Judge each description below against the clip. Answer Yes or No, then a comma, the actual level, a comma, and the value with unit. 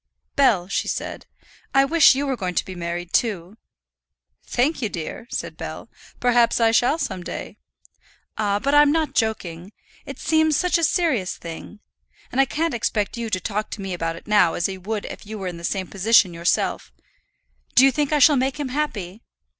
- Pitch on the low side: No, high, 220 Hz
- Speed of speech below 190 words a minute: No, average, 195 wpm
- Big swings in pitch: Yes, wide, 6.7 semitones